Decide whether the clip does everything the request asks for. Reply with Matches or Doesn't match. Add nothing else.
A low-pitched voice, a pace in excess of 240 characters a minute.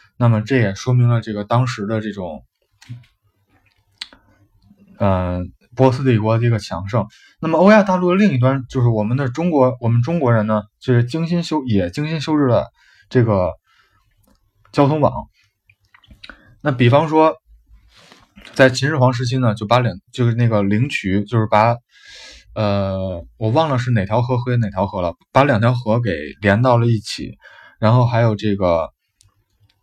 Doesn't match